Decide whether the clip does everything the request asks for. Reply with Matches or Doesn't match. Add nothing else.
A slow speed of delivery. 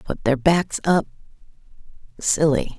Matches